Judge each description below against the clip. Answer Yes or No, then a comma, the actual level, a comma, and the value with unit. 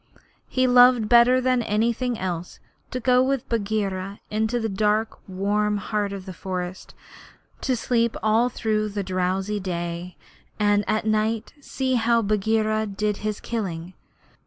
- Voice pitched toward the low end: No, high, 215 Hz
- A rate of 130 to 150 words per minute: Yes, average, 140 wpm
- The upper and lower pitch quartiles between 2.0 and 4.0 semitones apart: Yes, average, 3.0 semitones